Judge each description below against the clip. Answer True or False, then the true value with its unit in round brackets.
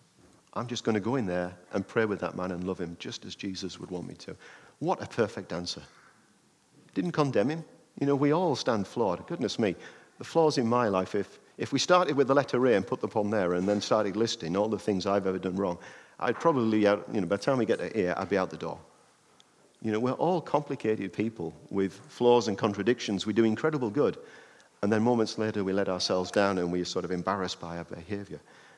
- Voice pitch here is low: True (100 Hz)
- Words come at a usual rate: False (235 wpm)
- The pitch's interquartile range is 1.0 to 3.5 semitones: False (4.6 semitones)